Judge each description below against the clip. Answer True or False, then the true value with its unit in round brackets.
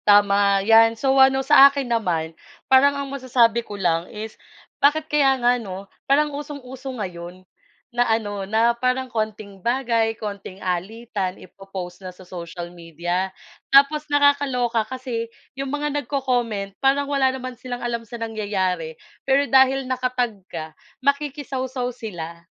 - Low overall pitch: False (235 Hz)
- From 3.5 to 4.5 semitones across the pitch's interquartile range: False (5.2 semitones)